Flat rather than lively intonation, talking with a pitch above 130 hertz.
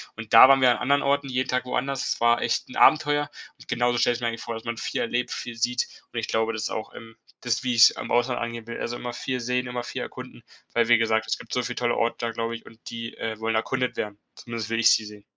No: narrow, 1.6 semitones; low, 120 Hz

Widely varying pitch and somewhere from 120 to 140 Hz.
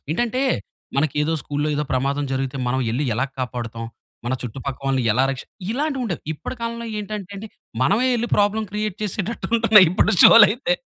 No: wide, 8.7 semitones; medium, 175 Hz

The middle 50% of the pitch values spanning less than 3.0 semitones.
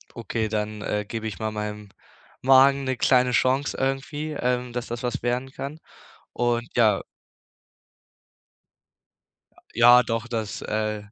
No: average, 3.3 semitones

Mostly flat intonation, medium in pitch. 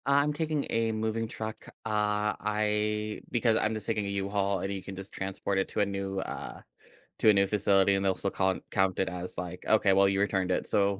No: narrow, 1.9 semitones; low, 100 Hz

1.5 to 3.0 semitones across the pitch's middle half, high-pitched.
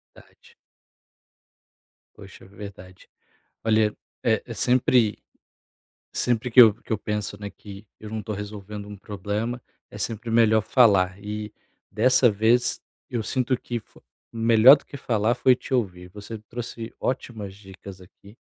No: narrow, 2.6 semitones; low, 110 Hz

